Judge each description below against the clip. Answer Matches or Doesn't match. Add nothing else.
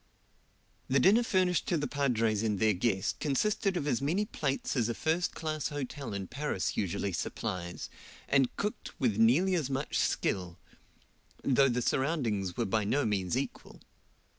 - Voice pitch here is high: Doesn't match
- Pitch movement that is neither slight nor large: Doesn't match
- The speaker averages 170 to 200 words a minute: Doesn't match